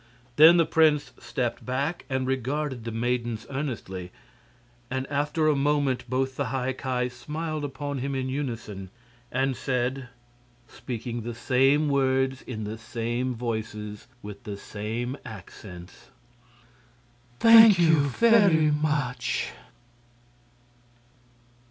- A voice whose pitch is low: Yes, low, 130 Hz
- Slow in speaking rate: Yes, slow, 115 wpm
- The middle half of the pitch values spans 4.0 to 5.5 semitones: No, average, 3.6 semitones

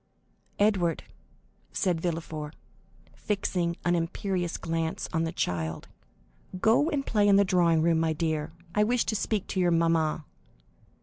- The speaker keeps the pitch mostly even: No, average, 3.6 semitones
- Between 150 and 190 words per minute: No, average, 140 wpm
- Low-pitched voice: No, medium, 170 Hz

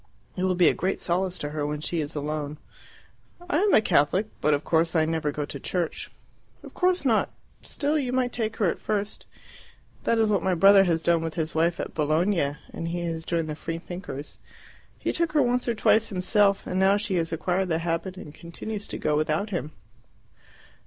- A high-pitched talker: No, medium, 175 Hz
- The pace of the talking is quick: Yes, fast, 210 wpm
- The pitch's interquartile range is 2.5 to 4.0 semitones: No, average, 4.4 semitones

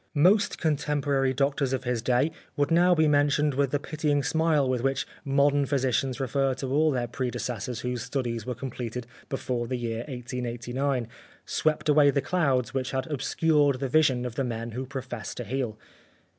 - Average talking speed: Yes, average, 175 wpm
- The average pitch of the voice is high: No, low, 135 Hz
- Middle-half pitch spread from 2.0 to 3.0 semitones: Yes, narrow, 2.6 semitones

